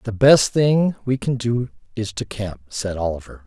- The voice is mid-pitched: No, low, 115 Hz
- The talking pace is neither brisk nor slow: Yes, average, 190 wpm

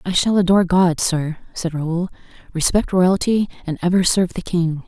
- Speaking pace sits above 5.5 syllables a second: No, 5.0 syllables/s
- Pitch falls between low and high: Yes, medium, 175 Hz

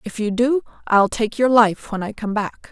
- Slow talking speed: No, fast, 245 wpm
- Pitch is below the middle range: No, high, 225 Hz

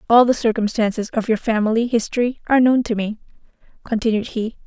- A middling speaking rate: Yes, average, 165 wpm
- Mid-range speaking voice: No, high, 225 Hz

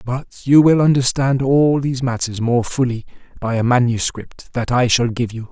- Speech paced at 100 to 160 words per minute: No, average, 185 wpm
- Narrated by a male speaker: Yes, male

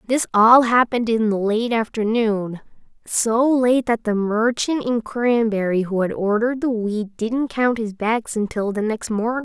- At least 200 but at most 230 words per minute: No, average, 170 wpm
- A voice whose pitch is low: No, high, 225 Hz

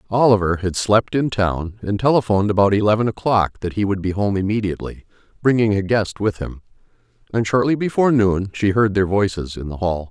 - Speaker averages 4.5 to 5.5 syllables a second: No, 5.7 syllables/s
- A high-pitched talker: No, low, 105 Hz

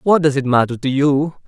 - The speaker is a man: Yes, male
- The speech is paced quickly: Yes, fast, 245 wpm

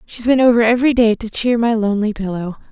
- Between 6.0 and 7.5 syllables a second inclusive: Yes, 6.5 syllables/s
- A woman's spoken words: Yes, female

